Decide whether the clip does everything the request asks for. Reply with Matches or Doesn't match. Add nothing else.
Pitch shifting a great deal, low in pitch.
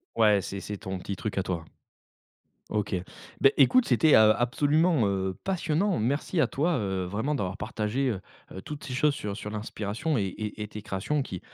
Matches